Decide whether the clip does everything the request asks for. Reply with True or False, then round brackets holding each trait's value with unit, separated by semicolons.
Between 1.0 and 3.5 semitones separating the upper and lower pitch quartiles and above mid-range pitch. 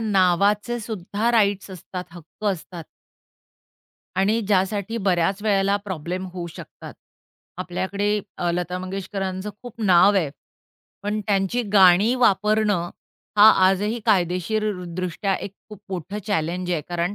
True (2.6 semitones; 195 Hz)